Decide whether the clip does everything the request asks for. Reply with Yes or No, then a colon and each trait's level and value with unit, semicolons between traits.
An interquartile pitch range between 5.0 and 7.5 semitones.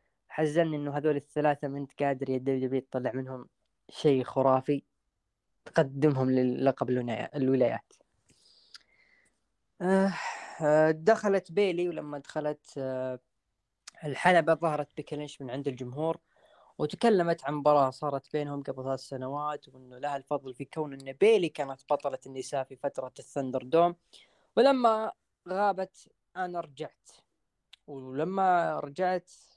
No: average, 3.6 semitones